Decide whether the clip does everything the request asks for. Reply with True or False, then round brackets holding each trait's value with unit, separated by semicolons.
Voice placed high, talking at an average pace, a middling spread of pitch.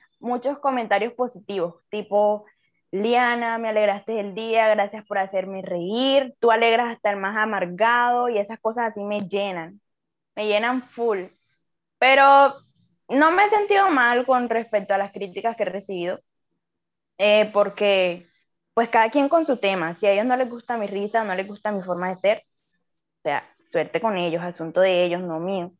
True (210 Hz; 175 wpm; 3.7 semitones)